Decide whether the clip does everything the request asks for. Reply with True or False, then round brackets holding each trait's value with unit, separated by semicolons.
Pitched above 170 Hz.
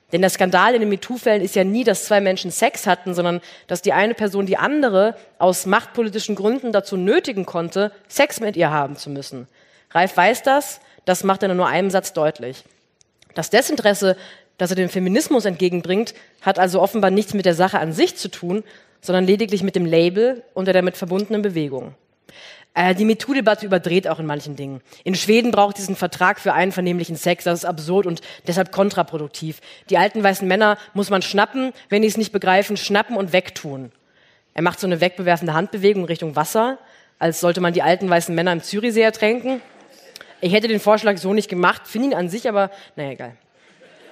True (190 Hz)